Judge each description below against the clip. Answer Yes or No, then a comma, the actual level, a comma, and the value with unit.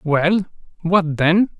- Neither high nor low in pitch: Yes, medium, 175 Hz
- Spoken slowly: Yes, slow, 115 wpm